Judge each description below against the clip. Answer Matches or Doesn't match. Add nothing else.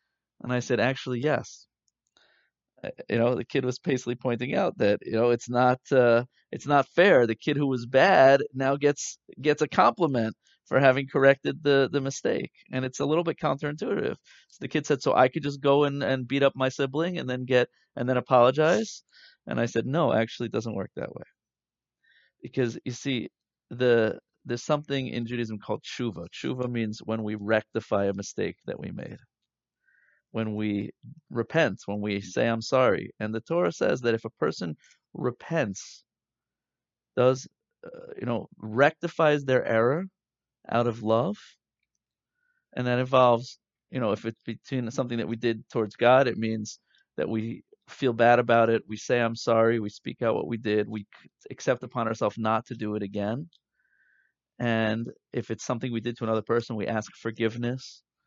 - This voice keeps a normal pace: Matches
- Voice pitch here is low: Matches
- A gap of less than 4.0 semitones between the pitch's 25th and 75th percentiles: Matches